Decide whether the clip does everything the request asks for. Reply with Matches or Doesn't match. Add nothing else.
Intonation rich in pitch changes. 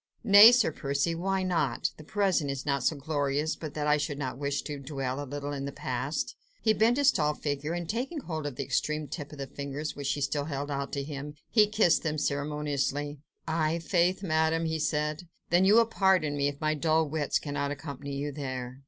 Doesn't match